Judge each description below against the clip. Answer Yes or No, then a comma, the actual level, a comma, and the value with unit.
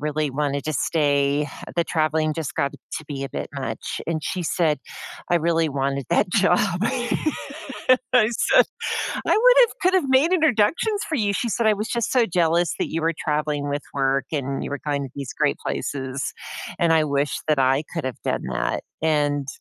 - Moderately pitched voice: Yes, medium, 155 Hz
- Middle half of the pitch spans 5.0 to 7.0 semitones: Yes, wide, 5.6 semitones